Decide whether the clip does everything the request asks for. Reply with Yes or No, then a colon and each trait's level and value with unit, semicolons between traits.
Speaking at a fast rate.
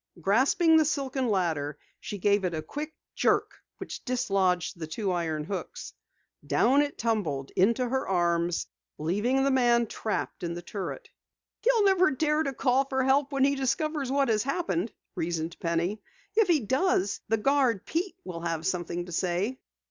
No: average, 165 wpm